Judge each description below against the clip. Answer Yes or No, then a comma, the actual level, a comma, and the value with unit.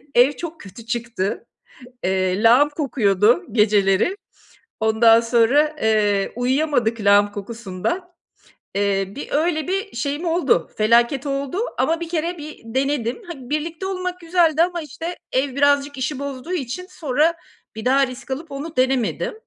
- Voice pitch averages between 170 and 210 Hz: No, very high, 270 Hz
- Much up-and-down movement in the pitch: Yes, wide, 5.8 semitones